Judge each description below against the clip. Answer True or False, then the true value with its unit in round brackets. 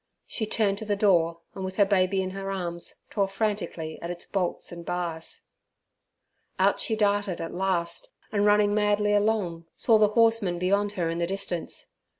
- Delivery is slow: False (175 wpm)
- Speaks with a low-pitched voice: False (195 Hz)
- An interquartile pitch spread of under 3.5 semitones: True (3.0 semitones)